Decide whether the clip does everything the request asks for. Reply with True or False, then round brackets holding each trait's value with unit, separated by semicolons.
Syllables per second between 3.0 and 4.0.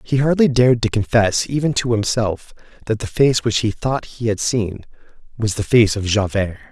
False (5.0 syllables/s)